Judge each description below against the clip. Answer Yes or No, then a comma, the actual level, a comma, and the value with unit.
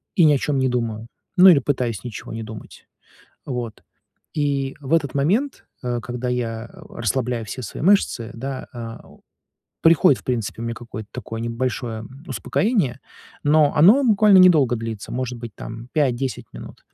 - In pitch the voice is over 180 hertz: No, low, 125 Hz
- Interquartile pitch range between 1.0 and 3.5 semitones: No, average, 4.0 semitones